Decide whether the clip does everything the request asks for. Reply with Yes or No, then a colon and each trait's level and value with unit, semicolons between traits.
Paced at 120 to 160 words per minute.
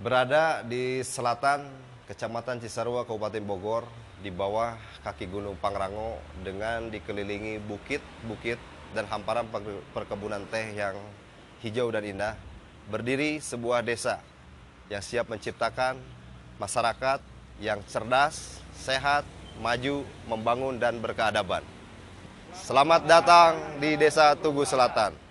No: average, 100 wpm